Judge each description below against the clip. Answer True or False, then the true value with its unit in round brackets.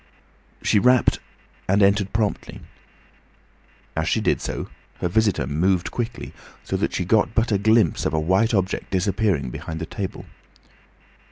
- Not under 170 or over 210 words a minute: False (150 wpm)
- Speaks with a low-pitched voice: True (100 Hz)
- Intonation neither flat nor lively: True (4.1 semitones)